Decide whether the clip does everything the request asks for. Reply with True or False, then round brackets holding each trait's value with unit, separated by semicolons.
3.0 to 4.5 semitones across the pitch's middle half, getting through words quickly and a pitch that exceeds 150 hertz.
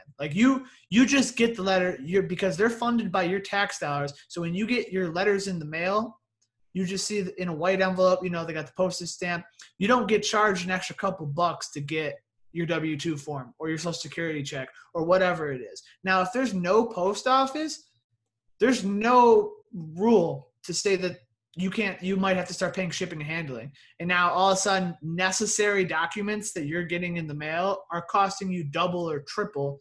True (3.6 semitones; 210 wpm; 185 Hz)